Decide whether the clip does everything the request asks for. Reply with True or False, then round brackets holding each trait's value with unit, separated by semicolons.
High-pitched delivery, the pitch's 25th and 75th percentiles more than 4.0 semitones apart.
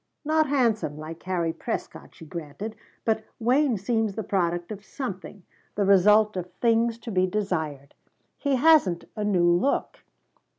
True (205 Hz; 4.7 semitones)